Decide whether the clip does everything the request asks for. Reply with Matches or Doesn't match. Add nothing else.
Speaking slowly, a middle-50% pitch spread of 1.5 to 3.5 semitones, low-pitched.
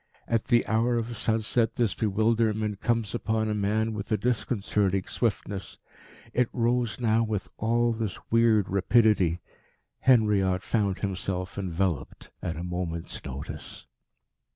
Matches